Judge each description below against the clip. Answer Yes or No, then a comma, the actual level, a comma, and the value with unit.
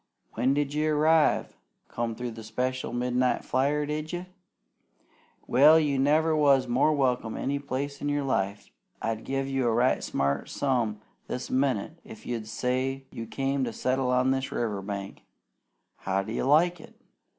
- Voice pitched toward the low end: Yes, low, 130 Hz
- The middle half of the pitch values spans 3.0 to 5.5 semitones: Yes, average, 3.5 semitones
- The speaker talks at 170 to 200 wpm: No, average, 160 wpm